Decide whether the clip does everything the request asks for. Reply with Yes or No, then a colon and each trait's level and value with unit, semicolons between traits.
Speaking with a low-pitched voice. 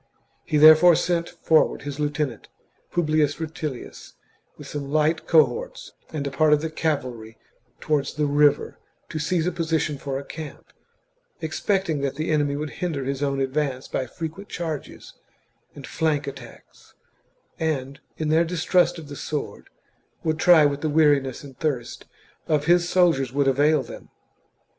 No: medium, 150 Hz